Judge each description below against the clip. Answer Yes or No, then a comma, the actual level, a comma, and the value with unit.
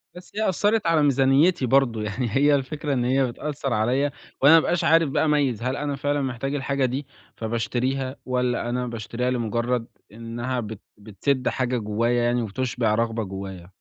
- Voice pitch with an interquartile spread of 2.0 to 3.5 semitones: Yes, average, 3.2 semitones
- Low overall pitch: Yes, low, 125 Hz